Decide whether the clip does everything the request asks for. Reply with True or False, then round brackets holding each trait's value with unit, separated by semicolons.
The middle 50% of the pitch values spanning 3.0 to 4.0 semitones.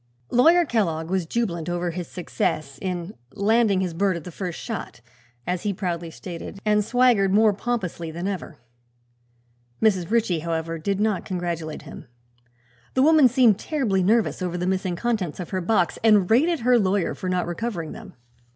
False (4.4 semitones)